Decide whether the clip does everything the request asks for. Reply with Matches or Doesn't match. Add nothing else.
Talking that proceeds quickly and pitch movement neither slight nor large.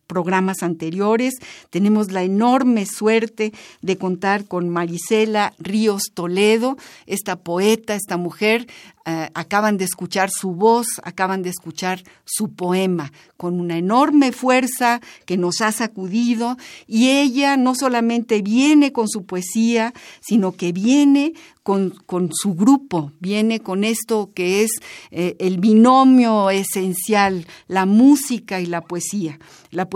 Doesn't match